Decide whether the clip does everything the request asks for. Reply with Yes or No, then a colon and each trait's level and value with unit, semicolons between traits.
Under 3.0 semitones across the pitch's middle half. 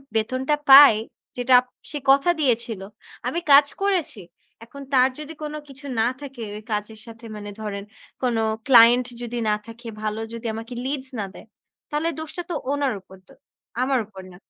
No: average, 4.0 semitones